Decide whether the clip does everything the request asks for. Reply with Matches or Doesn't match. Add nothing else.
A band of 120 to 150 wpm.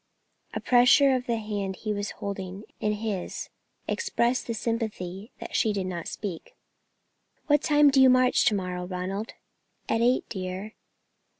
Doesn't match